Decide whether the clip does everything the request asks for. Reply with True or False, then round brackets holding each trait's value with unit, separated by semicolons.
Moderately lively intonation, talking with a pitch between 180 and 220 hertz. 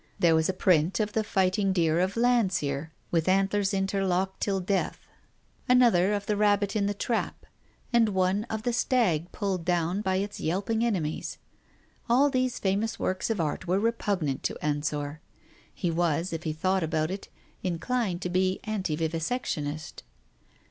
True (4.0 semitones; 190 Hz)